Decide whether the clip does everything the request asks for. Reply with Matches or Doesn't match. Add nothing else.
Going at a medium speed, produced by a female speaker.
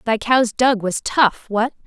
Matches